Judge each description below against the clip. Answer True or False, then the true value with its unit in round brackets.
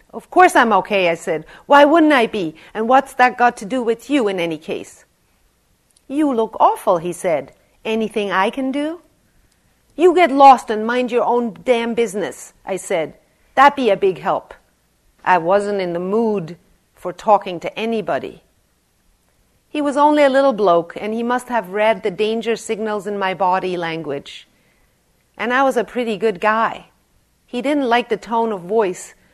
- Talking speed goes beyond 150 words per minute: True (180 wpm)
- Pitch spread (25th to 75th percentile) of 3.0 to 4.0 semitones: False (4.6 semitones)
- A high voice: True (220 Hz)